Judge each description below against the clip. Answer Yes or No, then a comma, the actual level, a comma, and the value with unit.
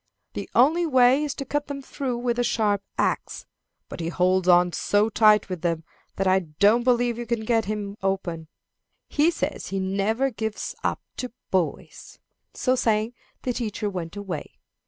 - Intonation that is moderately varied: Yes, average, 4.4 semitones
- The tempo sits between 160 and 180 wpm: Yes, average, 175 wpm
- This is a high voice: Yes, high, 215 Hz